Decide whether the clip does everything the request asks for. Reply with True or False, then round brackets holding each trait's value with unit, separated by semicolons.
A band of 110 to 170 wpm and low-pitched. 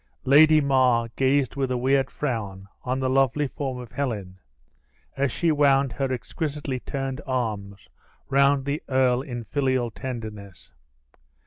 True (135 wpm; 130 Hz)